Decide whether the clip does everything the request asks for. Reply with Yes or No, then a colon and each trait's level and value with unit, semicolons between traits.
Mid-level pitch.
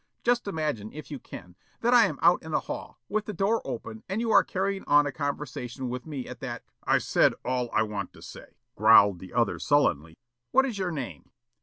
Yes: medium, 145 Hz